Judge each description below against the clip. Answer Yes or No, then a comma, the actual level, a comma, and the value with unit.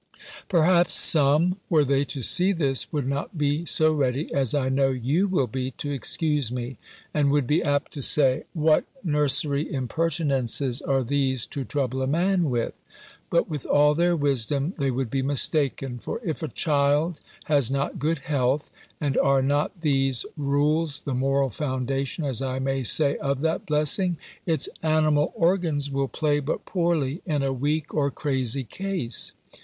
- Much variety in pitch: No, average, 2.7 semitones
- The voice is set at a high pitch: No, medium, 145 Hz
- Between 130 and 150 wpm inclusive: No, average, 165 wpm